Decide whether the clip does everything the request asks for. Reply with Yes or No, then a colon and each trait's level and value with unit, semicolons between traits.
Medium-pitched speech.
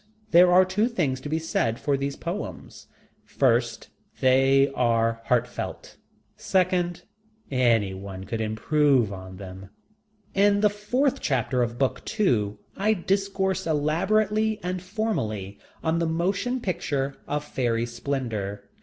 Yes: medium, 145 Hz